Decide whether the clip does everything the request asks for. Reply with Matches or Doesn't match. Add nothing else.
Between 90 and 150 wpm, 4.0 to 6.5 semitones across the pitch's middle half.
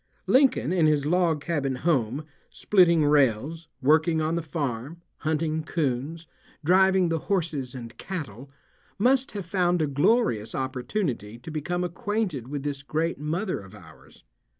Matches